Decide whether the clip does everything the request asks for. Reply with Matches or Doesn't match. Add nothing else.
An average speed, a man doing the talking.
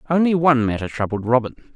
Matches